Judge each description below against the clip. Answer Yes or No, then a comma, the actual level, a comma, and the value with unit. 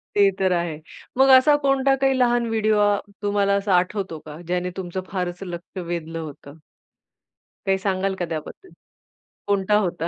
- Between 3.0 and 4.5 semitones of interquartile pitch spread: Yes, average, 3.3 semitones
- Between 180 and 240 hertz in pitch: Yes, high, 190 Hz